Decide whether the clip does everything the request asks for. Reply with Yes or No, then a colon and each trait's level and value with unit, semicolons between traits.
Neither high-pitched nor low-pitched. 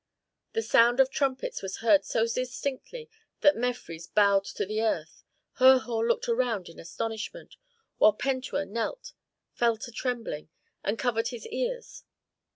No: high, 235 Hz